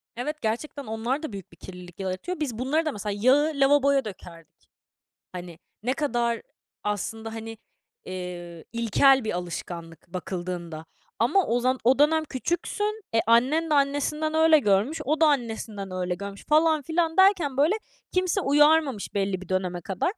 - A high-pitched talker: Yes, high, 240 Hz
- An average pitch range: No, wide, 7.9 semitones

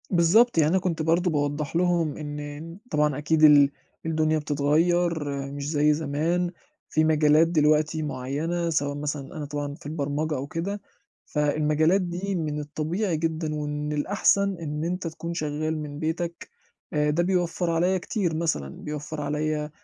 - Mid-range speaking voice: Yes, medium, 155 Hz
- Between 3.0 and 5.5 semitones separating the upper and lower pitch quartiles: No, narrow, 2.4 semitones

